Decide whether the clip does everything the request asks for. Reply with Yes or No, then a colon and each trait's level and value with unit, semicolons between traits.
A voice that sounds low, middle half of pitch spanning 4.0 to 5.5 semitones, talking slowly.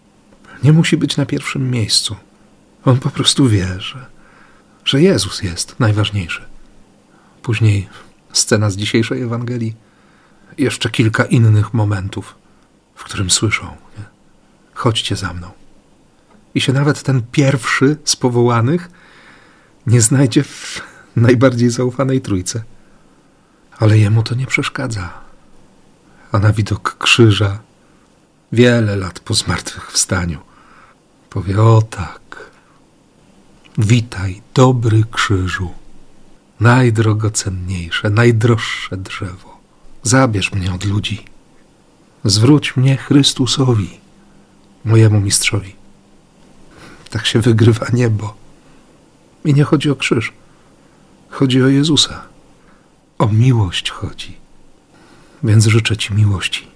Yes: low, 115 Hz; average, 4.3 semitones; slow, 100 wpm